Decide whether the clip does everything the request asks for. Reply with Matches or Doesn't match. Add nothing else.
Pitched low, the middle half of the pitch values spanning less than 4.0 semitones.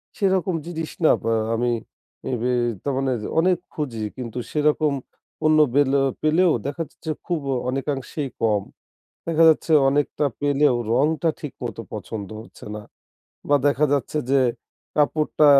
Doesn't match